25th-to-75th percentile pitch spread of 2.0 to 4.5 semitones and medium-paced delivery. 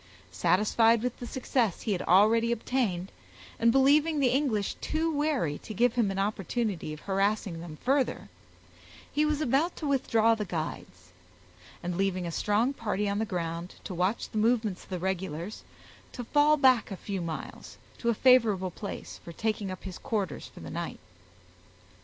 No: average, 5.2 semitones; average, 170 wpm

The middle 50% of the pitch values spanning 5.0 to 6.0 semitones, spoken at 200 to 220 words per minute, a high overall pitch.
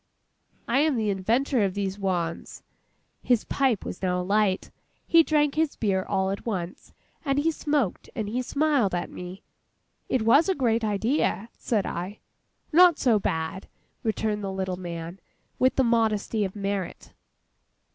No: average, 5.3 semitones; average, 155 wpm; high, 210 Hz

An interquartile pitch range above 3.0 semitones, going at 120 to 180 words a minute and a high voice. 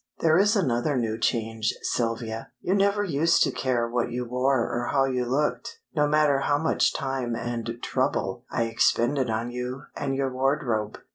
No: average, 3.5 semitones; average, 170 wpm; low, 125 Hz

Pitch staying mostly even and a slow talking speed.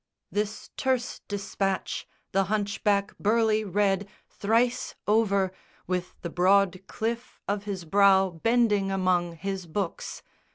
Yes: narrow, 2.1 semitones; slow, 115 wpm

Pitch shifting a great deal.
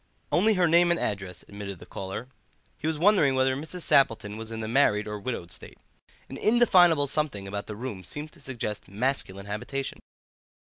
Yes: wide, 7.1 semitones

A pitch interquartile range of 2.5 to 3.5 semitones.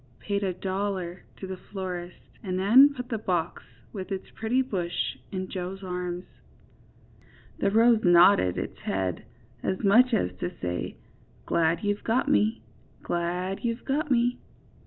No: average, 4.0 semitones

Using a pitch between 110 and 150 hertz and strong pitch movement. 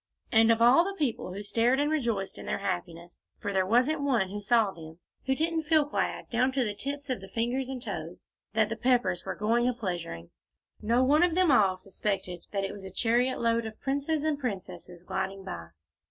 No: high, 230 Hz; wide, 5.7 semitones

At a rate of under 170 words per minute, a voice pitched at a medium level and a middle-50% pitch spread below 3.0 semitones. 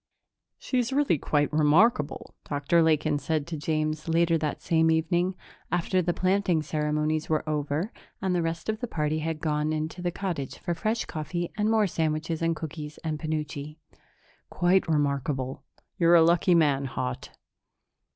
Yes: average, 155 wpm; medium, 160 Hz; narrow, 2.4 semitones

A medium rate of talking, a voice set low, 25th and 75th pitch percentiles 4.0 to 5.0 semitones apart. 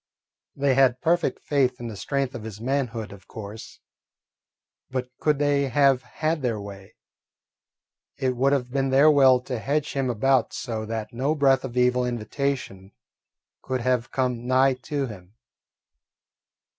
No: average, 150 wpm; low, 130 Hz; average, 2.9 semitones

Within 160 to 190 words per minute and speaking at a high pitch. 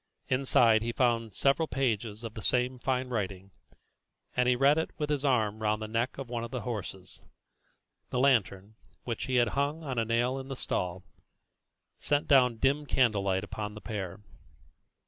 No: average, 175 wpm; low, 120 Hz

